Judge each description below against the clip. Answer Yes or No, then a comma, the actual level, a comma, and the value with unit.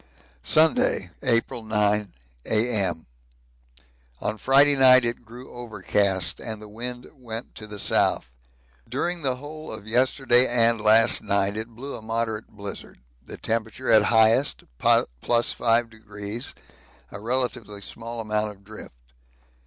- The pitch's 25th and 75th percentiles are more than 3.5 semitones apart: No, narrow, 2.6 semitones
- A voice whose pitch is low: Yes, low, 115 Hz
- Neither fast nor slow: No, slow, 125 wpm